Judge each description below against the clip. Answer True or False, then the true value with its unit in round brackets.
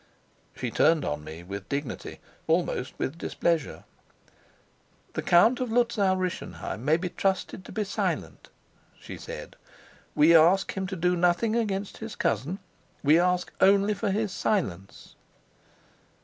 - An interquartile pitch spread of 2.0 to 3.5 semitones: False (4.2 semitones)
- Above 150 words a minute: False (135 wpm)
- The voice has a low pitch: False (180 Hz)